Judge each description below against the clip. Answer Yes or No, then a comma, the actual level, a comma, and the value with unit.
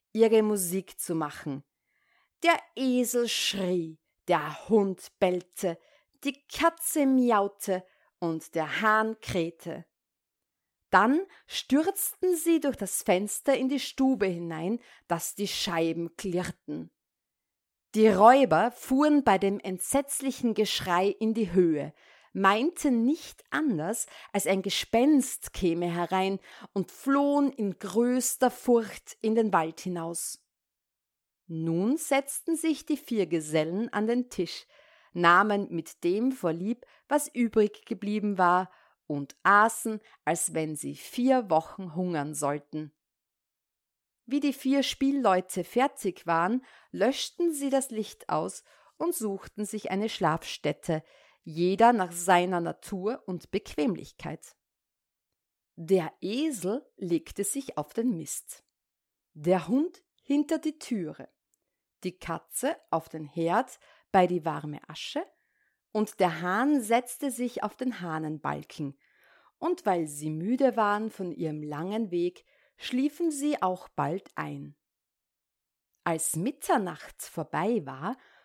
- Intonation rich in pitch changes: Yes, wide, 6.8 semitones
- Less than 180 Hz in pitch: No, high, 200 Hz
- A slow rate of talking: Yes, slow, 115 wpm